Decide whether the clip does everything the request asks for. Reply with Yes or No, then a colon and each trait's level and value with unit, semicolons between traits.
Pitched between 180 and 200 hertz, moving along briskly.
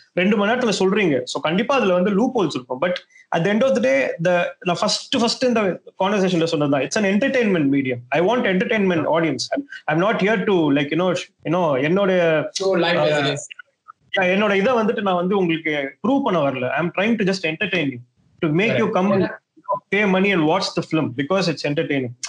Yes: medium, 185 Hz; fast, 135 wpm